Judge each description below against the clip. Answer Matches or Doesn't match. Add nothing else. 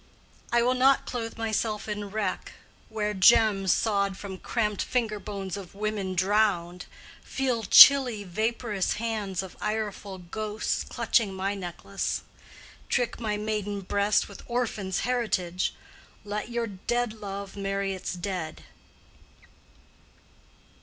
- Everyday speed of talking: Doesn't match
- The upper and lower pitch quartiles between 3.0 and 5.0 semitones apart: Doesn't match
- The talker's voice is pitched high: Matches